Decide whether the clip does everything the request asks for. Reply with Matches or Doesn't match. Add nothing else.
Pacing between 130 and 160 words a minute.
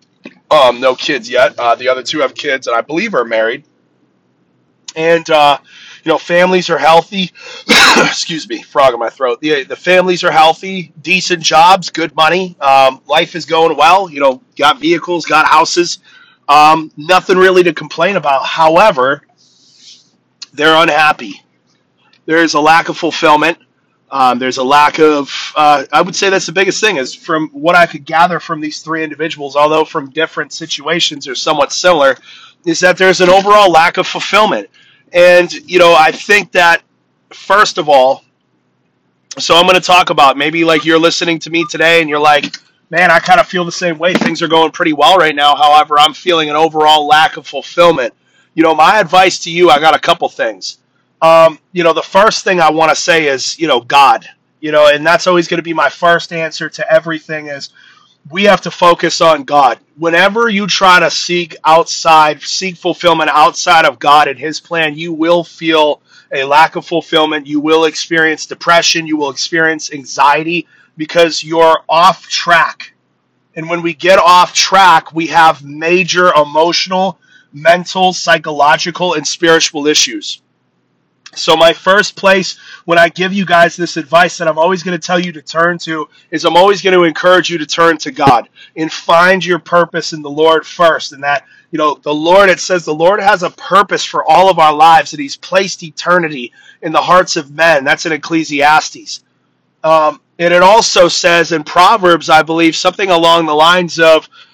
Doesn't match